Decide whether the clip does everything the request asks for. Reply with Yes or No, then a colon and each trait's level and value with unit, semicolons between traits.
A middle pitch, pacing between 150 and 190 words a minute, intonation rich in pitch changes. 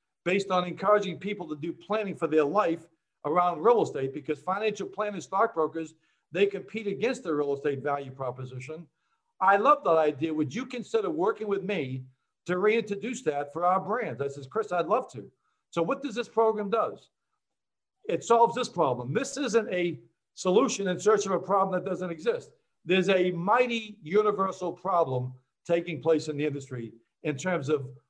Yes: medium, 180 Hz; average, 175 wpm; wide, 5.8 semitones